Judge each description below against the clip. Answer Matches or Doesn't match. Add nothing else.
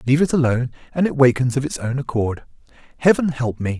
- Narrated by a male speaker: Matches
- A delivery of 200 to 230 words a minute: Matches